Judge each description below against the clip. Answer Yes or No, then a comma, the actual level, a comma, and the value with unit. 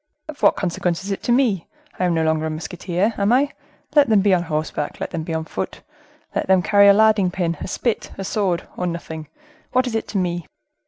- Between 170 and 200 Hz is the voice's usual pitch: Yes, medium, 185 Hz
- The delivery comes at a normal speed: No, fast, 225 wpm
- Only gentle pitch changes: No, average, 4.4 semitones